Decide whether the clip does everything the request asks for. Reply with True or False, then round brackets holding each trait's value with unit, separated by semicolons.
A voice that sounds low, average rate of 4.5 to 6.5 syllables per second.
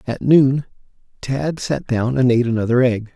True (125 Hz; 4.9 syllables/s)